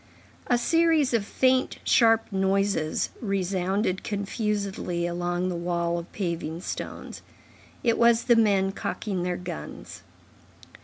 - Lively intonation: No, average, 4.3 semitones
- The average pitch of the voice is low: No, high, 195 Hz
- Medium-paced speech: No, slow, 115 wpm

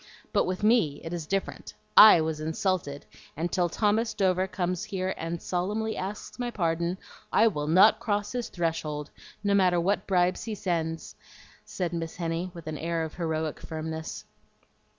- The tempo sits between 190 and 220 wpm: No, average, 165 wpm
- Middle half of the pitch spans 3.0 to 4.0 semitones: Yes, average, 3.6 semitones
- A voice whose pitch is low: No, medium, 175 Hz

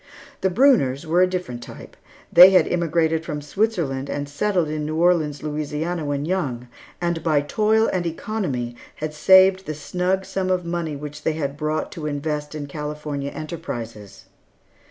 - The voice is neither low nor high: Yes, medium, 155 Hz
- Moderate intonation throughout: Yes, average, 3.6 semitones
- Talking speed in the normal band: Yes, average, 155 wpm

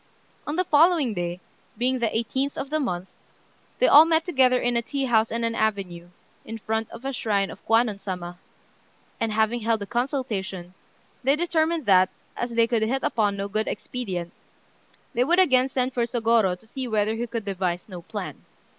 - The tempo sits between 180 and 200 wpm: Yes, average, 190 wpm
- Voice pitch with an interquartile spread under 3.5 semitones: No, average, 4.5 semitones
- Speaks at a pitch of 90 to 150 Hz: No, high, 230 Hz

